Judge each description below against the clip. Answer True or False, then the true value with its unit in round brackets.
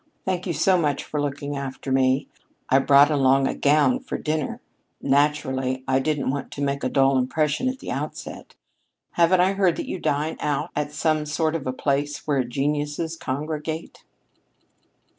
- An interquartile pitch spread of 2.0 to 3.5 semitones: True (2.5 semitones)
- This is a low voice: False (145 Hz)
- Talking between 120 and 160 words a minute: False (170 wpm)